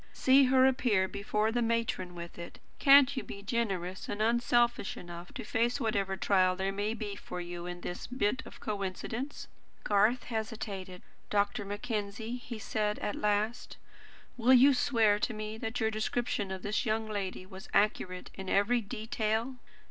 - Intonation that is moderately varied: Yes, average, 3.3 semitones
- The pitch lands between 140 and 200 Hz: No, high, 215 Hz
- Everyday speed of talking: Yes, average, 165 wpm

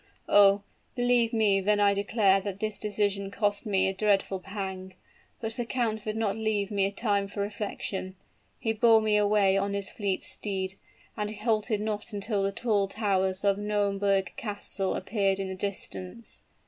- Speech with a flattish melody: Yes, narrow, 1.5 semitones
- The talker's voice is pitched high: Yes, high, 205 Hz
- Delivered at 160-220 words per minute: Yes, average, 165 wpm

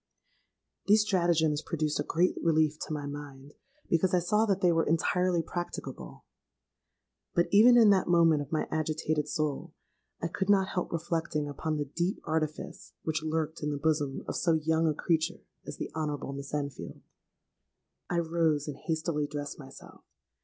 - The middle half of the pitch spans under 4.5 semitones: Yes, narrow, 2.5 semitones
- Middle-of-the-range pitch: Yes, medium, 160 Hz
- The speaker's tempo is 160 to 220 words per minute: Yes, average, 165 wpm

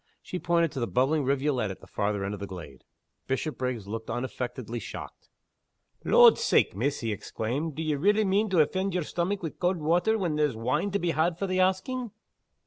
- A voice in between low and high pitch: Yes, medium, 150 Hz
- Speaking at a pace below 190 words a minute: No, average, 195 wpm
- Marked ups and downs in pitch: Yes, wide, 7.2 semitones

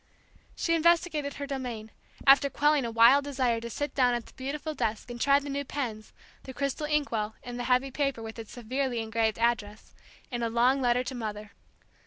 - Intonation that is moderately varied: Yes, average, 3.5 semitones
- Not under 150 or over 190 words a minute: No, average, 200 wpm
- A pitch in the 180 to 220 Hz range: No, very high, 250 Hz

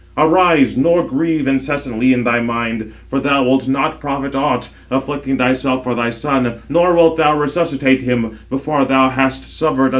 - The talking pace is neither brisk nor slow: Yes, average, 175 wpm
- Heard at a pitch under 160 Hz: Yes, low, 135 Hz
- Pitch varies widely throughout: No, narrow, 2.5 semitones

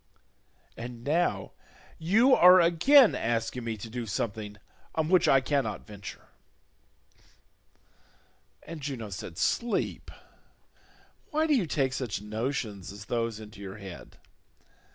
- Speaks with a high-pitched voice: No, low, 120 Hz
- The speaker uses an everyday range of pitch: No, wide, 7.6 semitones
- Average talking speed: No, slow, 120 wpm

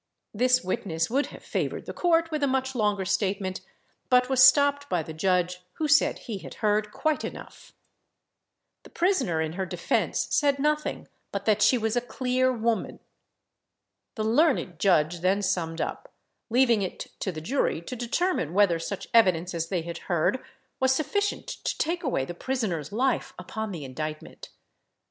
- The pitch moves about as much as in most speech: No, wide, 6.8 semitones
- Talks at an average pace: Yes, average, 165 wpm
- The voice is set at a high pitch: Yes, high, 215 Hz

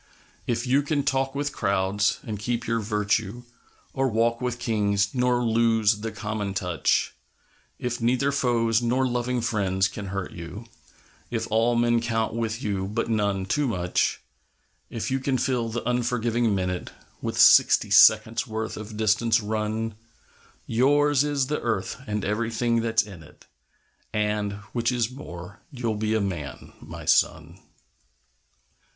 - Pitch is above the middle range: No, low, 115 Hz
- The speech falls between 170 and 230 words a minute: No, average, 145 wpm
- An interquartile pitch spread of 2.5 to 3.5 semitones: Yes, average, 2.8 semitones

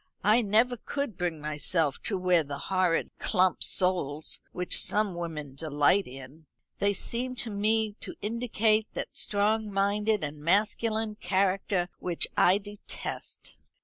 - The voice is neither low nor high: No, high, 195 Hz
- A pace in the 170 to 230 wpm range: No, slow, 135 wpm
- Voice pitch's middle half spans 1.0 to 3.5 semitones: No, average, 4.4 semitones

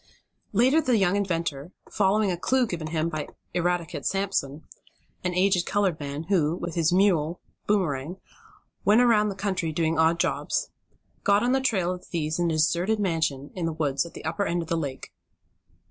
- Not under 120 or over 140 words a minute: No, average, 185 wpm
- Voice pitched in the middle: Yes, medium, 175 Hz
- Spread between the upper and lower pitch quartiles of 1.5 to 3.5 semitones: No, average, 3.9 semitones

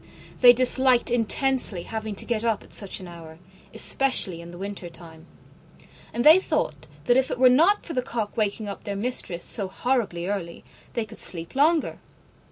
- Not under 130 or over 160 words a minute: No, average, 175 wpm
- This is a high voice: Yes, high, 220 Hz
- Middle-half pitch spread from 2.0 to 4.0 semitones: No, wide, 5.5 semitones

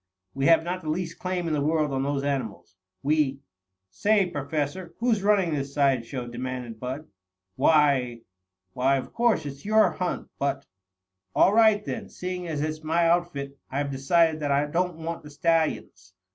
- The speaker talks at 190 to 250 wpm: No, average, 175 wpm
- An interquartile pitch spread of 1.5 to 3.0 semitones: No, average, 4.1 semitones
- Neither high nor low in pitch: Yes, medium, 150 Hz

